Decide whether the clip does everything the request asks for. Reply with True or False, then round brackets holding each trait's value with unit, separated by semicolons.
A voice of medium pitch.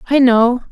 False (250 Hz)